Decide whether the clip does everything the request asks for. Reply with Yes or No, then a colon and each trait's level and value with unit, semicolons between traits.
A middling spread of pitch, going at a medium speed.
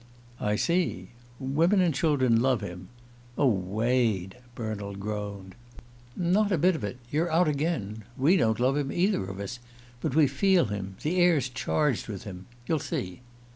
No: wide, 7.7 semitones; average, 165 wpm